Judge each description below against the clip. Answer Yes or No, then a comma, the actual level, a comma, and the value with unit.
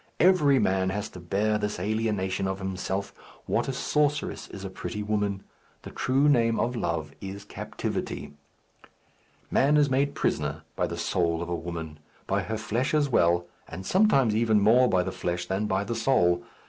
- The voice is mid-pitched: No, low, 105 Hz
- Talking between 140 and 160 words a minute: No, average, 175 wpm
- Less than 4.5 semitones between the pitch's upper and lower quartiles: No, average, 5.0 semitones